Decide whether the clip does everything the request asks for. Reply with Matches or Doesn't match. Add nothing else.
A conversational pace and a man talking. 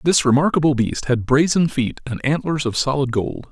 Matches